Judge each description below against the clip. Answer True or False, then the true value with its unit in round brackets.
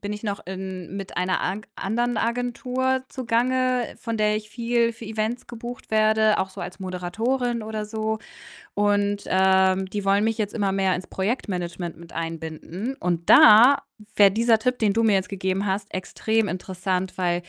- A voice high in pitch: True (210 Hz)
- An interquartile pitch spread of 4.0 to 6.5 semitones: False (3.4 semitones)